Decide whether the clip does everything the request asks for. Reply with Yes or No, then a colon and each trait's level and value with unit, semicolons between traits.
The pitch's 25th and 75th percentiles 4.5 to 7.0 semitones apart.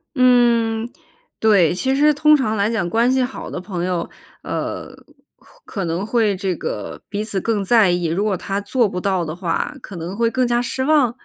Yes: average, 4.8 semitones